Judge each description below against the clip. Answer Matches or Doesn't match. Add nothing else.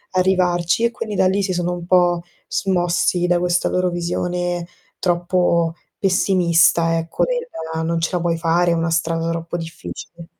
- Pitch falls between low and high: Matches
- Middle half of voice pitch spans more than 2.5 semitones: Doesn't match